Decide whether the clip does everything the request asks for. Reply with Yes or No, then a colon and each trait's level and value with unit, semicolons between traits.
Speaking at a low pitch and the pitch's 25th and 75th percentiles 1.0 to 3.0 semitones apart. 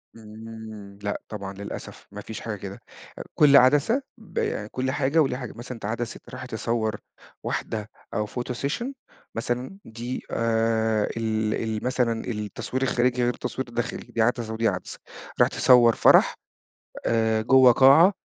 Yes: low, 115 Hz; narrow, 2.6 semitones